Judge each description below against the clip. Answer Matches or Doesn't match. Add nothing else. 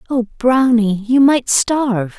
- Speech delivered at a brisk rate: Doesn't match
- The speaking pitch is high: Matches